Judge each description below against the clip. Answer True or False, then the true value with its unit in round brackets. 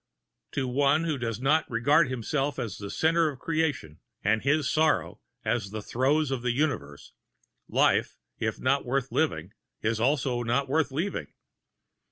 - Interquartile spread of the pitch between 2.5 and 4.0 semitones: False (4.6 semitones)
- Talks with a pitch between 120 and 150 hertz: True (135 Hz)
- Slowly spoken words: False (155 wpm)